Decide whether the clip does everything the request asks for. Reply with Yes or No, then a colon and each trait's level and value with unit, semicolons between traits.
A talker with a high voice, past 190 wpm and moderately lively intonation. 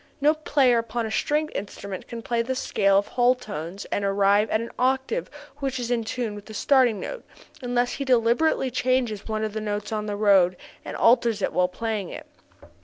Yes: high, 230 Hz; average, 200 wpm; average, 3.7 semitones